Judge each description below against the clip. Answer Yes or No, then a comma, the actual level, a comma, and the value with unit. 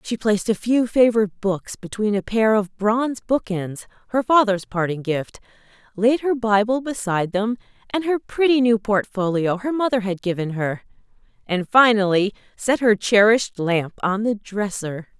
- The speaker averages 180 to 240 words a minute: No, average, 160 wpm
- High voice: Yes, high, 215 Hz